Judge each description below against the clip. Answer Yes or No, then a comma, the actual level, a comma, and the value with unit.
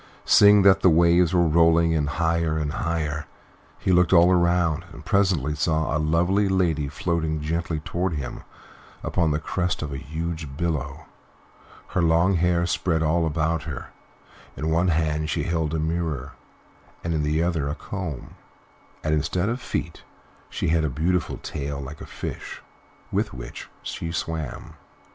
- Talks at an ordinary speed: Yes, average, 160 wpm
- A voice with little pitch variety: Yes, narrow, 2.2 semitones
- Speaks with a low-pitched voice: Yes, very low, 80 Hz